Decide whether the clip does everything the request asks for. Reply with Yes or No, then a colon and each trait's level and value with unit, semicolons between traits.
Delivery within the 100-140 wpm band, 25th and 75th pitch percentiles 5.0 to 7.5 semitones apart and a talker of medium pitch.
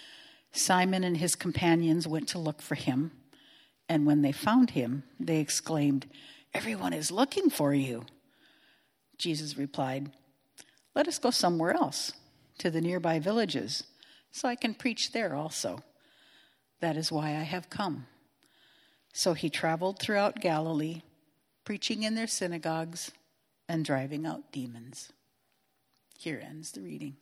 Yes: slow, 135 wpm; wide, 5.5 semitones; medium, 165 Hz